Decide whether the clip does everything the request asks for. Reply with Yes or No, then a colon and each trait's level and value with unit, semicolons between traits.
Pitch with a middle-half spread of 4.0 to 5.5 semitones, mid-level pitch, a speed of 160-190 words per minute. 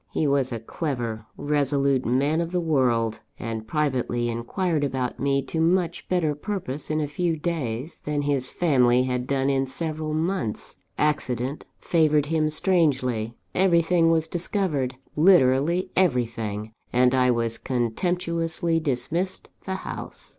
No: average, 4.7 semitones; medium, 145 Hz; slow, 135 wpm